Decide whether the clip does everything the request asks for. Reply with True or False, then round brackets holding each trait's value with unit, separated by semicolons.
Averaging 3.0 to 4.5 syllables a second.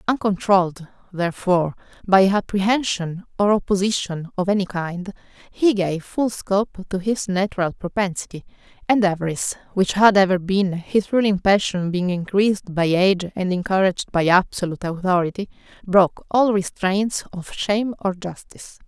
False (5.1 syllables/s)